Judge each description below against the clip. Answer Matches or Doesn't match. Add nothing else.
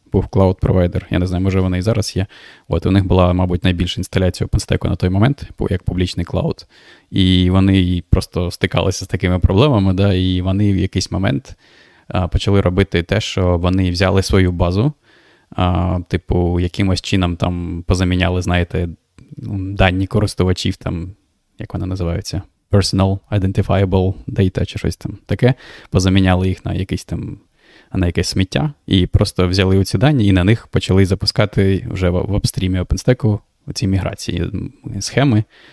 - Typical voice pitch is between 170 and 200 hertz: Doesn't match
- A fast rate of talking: Matches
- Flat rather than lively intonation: Matches